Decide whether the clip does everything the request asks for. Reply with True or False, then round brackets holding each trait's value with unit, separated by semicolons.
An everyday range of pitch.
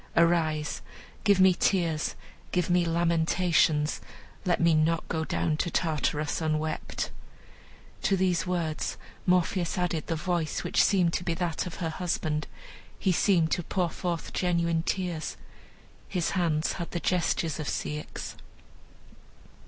False (2.1 semitones)